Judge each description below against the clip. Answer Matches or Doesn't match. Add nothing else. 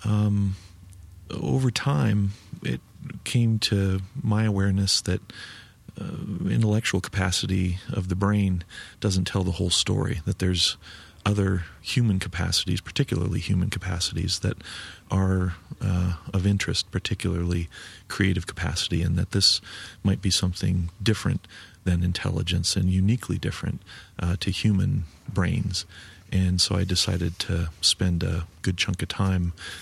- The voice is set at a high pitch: Doesn't match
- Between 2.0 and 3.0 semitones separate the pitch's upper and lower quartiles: Matches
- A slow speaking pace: Matches